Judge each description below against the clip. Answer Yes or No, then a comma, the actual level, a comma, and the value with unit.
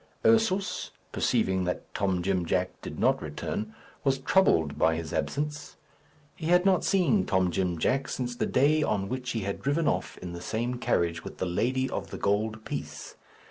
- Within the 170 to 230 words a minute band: Yes, average, 180 wpm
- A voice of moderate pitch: No, low, 110 Hz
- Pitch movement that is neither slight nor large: No, wide, 7.9 semitones